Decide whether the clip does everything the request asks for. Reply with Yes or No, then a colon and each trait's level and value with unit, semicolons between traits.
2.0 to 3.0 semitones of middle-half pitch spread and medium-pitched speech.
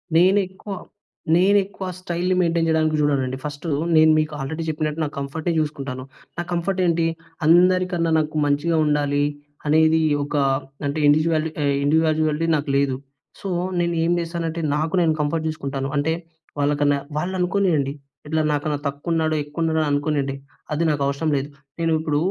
Yes: narrow, 2.4 semitones; medium, 155 Hz